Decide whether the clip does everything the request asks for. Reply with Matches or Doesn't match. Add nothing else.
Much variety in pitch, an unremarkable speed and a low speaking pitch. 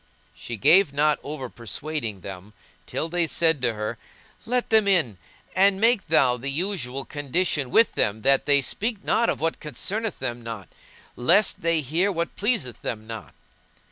Doesn't match